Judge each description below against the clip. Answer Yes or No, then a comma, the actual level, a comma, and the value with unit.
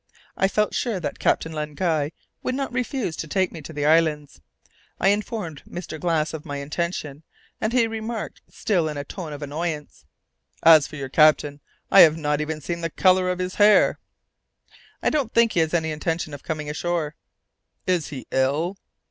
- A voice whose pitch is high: No, medium, 160 Hz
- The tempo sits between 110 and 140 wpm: No, average, 185 wpm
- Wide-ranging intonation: No, average, 3.8 semitones